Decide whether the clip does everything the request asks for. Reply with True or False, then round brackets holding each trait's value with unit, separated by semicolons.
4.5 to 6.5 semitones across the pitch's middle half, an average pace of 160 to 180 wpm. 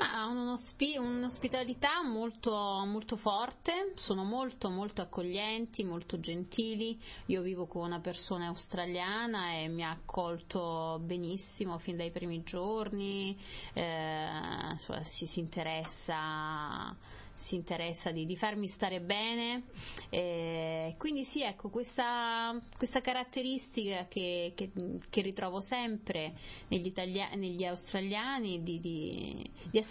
False (4.9 semitones; 120 wpm)